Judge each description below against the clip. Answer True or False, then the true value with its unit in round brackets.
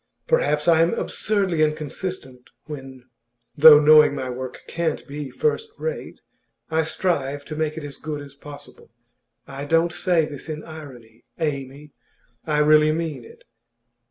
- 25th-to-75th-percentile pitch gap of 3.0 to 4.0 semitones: False (2.5 semitones)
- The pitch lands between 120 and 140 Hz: False (150 Hz)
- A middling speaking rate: True (145 wpm)